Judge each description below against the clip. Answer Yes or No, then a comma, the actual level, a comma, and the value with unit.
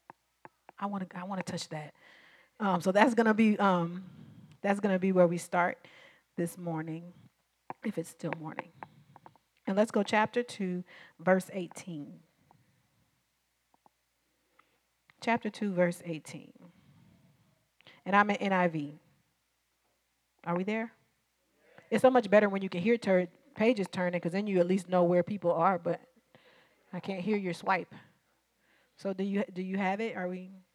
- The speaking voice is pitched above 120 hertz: Yes, medium, 185 Hz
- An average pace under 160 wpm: Yes, average, 150 wpm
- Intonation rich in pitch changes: No, average, 2.8 semitones